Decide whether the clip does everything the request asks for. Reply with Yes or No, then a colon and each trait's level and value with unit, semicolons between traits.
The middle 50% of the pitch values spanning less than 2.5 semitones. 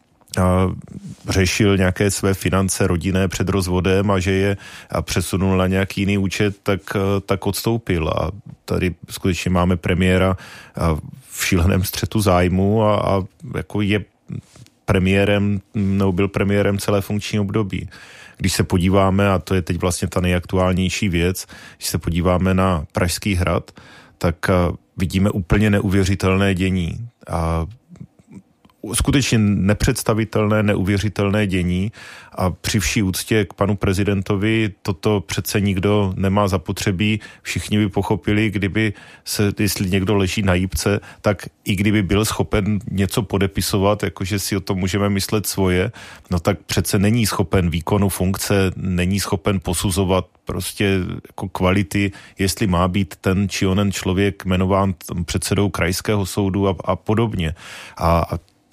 Yes: narrow, 1.8 semitones